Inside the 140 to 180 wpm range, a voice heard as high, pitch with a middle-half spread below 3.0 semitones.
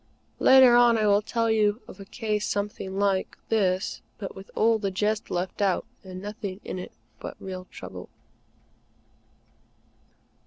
Yes: average, 150 wpm; high, 205 Hz; narrow, 2.4 semitones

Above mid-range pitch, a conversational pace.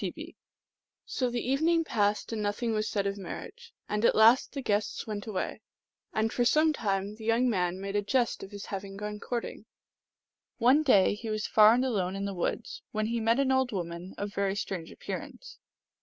No: high, 215 Hz; fast, 210 wpm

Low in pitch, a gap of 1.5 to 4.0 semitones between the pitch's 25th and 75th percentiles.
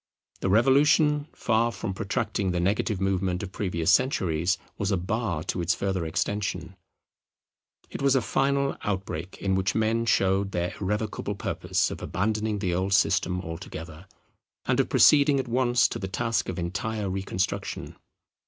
Yes: low, 100 Hz; average, 3.6 semitones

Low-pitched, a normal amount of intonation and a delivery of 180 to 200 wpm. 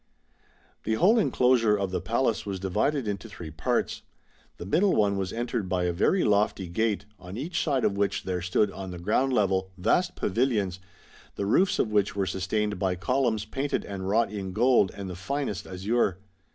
Yes: low, 105 Hz; average, 4.0 semitones; average, 185 wpm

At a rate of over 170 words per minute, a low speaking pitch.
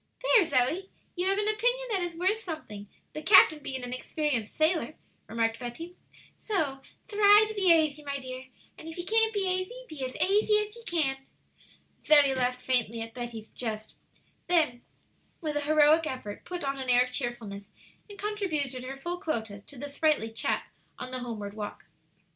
No: average, 180 wpm; very high, 295 Hz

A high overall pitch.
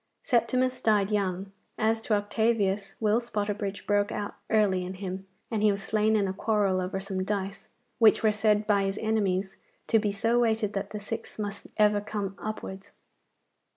Yes: high, 205 Hz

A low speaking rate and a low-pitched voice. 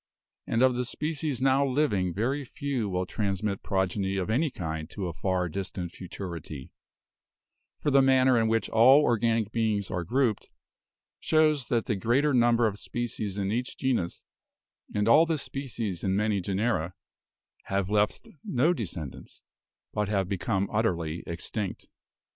No: average, 150 wpm; low, 110 Hz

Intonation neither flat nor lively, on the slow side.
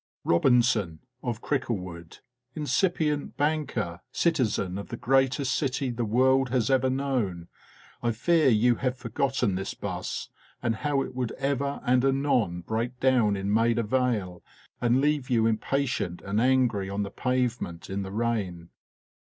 No: average, 4.3 semitones; average, 145 wpm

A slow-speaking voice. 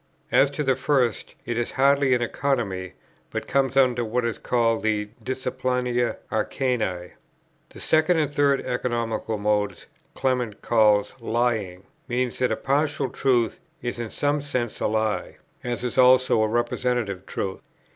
No: average, 145 wpm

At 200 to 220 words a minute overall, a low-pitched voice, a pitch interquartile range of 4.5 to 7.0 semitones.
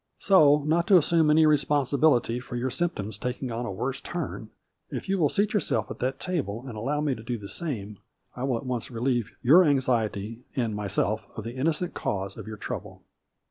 Yes: fast, 205 wpm; low, 125 Hz; average, 5.3 semitones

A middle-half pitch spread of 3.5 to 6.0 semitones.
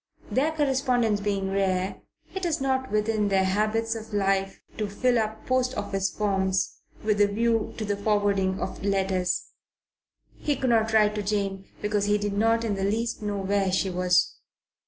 No: narrow, 2.6 semitones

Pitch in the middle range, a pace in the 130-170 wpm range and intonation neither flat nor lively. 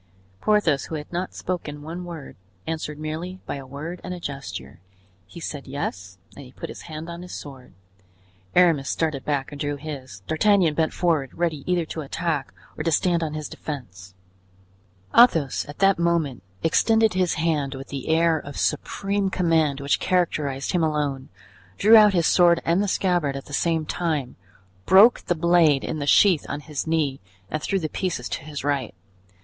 No: medium, 155 Hz; average, 180 wpm; average, 3.6 semitones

